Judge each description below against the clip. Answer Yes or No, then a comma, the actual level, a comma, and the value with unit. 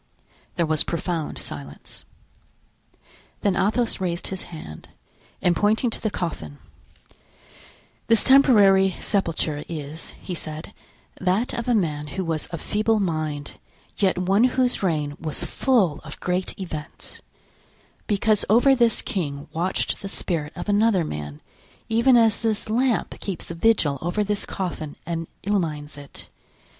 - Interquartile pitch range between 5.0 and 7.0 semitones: Yes, wide, 5.5 semitones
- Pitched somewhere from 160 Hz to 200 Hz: Yes, medium, 185 Hz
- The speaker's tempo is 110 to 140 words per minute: Yes, slow, 135 wpm